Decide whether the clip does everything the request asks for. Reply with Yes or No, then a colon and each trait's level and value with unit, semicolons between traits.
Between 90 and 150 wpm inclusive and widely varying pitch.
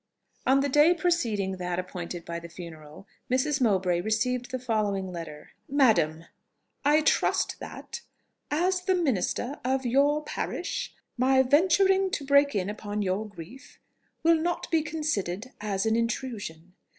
Yes: average, 140 wpm; wide, 7.6 semitones